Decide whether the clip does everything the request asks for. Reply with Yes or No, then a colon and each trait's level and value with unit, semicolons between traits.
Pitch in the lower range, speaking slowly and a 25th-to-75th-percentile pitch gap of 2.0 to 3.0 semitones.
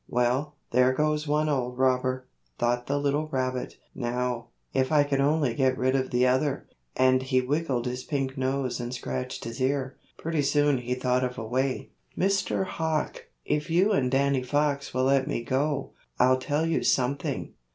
No: low, 130 Hz; average, 175 wpm; narrow, 2.4 semitones